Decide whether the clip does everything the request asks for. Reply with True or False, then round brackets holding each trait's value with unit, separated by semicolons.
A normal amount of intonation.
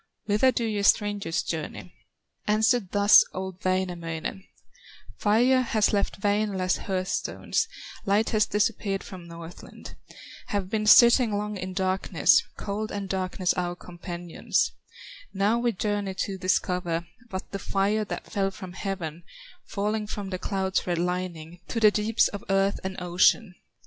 False (2.3 semitones)